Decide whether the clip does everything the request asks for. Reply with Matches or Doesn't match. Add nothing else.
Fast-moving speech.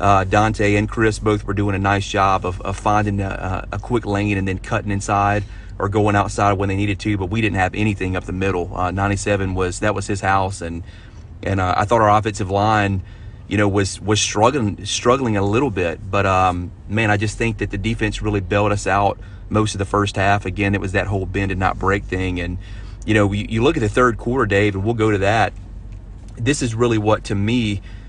Matches